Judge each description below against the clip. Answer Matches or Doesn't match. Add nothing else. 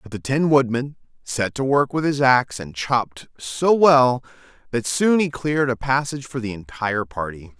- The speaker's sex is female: Doesn't match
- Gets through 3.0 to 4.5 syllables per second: Doesn't match